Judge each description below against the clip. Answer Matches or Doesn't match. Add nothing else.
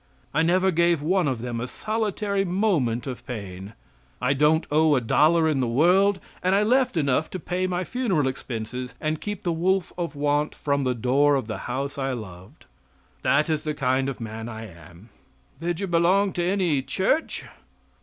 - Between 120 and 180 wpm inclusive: Doesn't match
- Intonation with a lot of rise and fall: Matches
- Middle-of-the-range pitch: Matches